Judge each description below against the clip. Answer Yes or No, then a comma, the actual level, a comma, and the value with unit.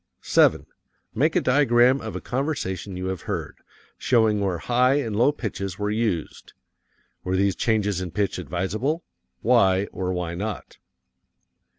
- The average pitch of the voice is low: Yes, low, 105 Hz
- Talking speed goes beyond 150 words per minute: No, average, 145 wpm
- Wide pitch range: No, average, 4.7 semitones